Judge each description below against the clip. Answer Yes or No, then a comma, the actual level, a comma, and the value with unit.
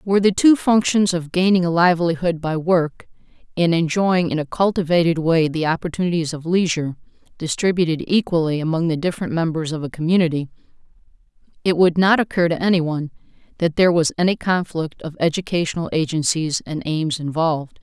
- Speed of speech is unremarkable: Yes, average, 160 wpm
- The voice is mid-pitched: Yes, medium, 170 Hz